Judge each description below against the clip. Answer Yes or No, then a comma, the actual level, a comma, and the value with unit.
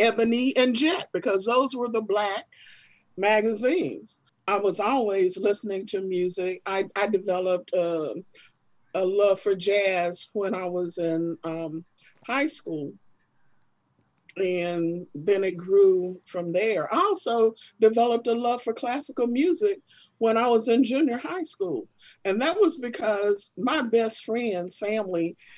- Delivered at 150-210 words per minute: No, average, 140 wpm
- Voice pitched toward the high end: Yes, high, 205 Hz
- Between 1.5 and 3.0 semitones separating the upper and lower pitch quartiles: No, average, 4.7 semitones